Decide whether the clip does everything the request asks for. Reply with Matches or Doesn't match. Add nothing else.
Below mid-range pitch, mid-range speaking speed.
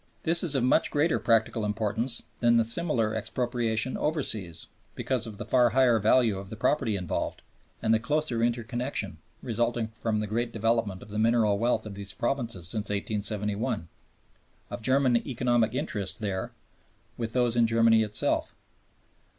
Matches